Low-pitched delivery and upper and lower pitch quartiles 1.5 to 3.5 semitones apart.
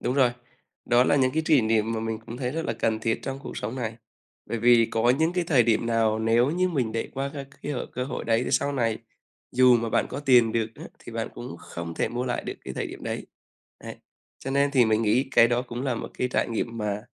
Yes: low, 120 Hz; average, 3.0 semitones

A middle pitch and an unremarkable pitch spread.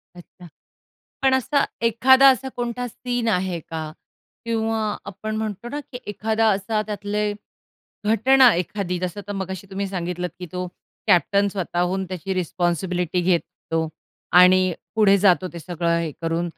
No: high, 195 Hz; average, 3.7 semitones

